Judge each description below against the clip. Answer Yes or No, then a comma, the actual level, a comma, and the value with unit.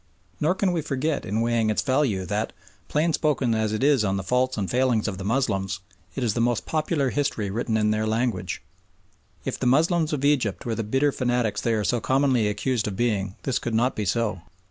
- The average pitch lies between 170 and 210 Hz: No, low, 120 Hz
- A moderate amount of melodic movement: Yes, average, 4.2 semitones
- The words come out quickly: Yes, fast, 215 wpm